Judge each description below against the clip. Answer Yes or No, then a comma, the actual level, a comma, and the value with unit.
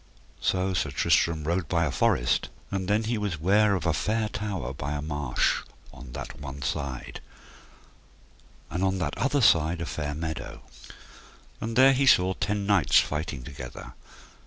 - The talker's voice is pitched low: Yes, very low, 85 Hz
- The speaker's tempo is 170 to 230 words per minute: No, average, 160 wpm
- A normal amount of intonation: No, wide, 5.8 semitones